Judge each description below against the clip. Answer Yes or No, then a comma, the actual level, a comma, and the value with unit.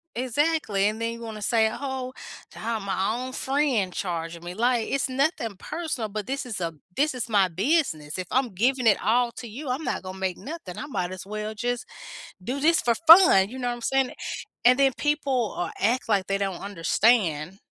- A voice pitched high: Yes, high, 230 Hz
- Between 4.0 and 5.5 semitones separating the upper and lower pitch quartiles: Yes, average, 5.2 semitones